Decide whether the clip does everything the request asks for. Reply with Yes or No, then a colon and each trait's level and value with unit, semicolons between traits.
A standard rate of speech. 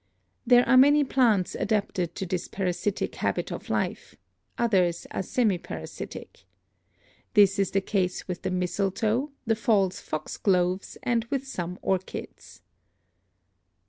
No: slow, 130 wpm